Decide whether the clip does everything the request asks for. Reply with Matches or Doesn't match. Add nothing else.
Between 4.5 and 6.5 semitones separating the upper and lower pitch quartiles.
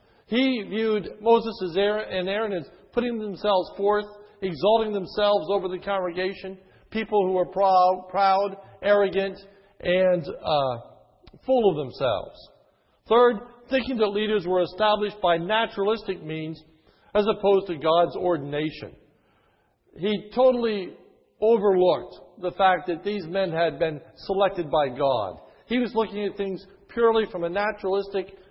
Doesn't match